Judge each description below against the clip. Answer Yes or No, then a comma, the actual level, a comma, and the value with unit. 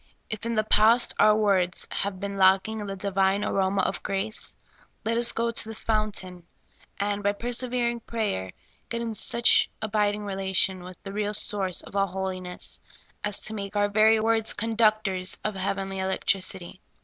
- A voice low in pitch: No, high, 205 Hz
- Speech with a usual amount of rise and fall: No, narrow, 2.3 semitones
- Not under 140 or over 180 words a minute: Yes, average, 165 wpm